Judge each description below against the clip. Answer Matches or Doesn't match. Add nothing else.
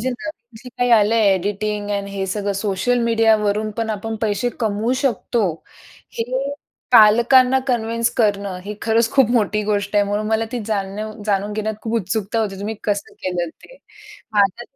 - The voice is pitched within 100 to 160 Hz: Doesn't match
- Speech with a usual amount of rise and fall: Doesn't match